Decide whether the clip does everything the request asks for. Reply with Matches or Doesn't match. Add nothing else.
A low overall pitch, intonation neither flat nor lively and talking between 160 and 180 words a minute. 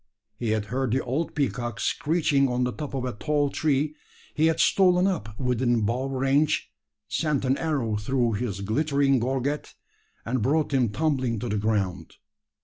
Matches